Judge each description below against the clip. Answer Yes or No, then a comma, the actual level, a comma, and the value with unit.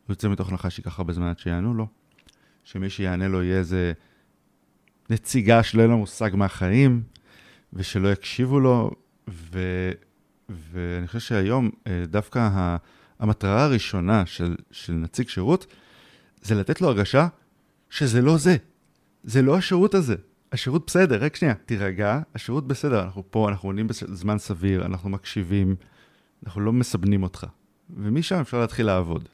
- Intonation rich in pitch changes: No, average, 4.6 semitones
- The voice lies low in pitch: Yes, low, 105 Hz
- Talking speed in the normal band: Yes, average, 140 wpm